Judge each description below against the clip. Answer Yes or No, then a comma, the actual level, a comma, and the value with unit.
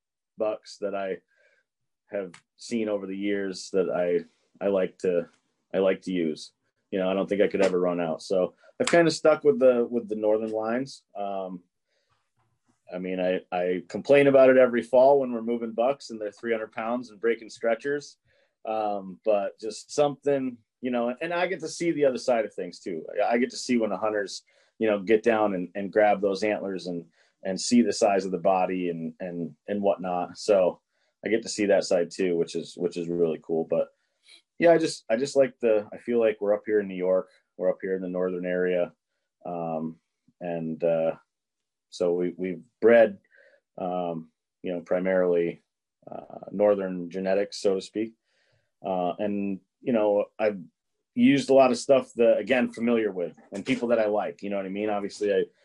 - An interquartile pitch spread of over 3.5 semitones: Yes, average, 4.5 semitones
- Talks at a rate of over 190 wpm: Yes, average, 200 wpm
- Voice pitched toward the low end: Yes, low, 100 Hz